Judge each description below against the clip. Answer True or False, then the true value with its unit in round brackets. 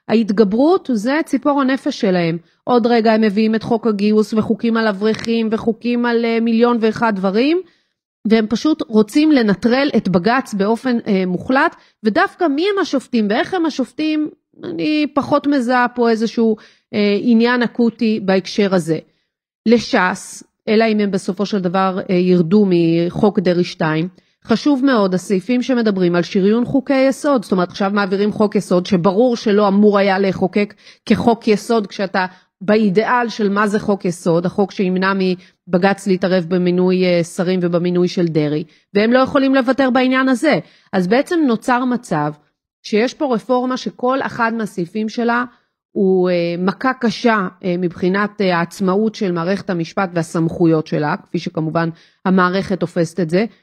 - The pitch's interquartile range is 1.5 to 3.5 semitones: False (4.6 semitones)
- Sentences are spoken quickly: False (140 wpm)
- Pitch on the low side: False (215 Hz)